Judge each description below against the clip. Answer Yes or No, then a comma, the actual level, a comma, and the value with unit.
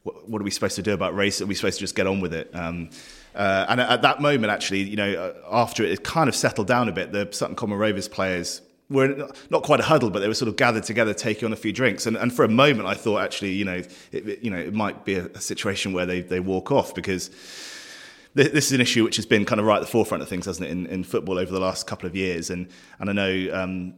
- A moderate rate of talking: No, fast, 285 wpm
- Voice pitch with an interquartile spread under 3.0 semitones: No, average, 3.3 semitones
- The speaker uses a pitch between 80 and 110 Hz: Yes, low, 100 Hz